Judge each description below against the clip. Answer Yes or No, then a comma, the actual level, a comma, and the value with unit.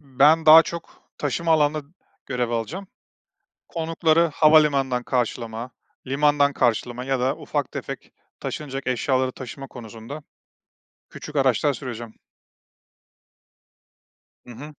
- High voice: No, low, 135 Hz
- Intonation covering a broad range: No, average, 3.7 semitones